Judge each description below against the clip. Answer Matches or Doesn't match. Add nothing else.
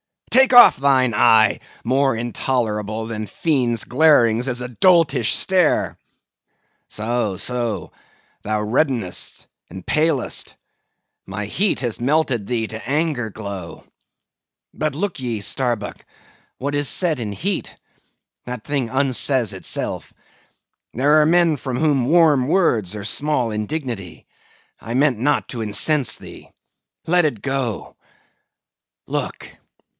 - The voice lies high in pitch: Doesn't match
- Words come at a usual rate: Doesn't match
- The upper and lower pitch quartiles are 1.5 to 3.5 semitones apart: Doesn't match